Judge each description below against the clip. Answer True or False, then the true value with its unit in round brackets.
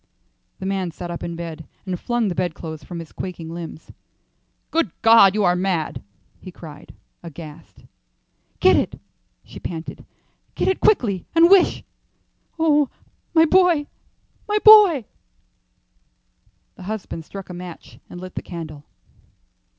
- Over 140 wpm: False (135 wpm)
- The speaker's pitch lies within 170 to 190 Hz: True (185 Hz)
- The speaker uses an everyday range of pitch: False (6.4 semitones)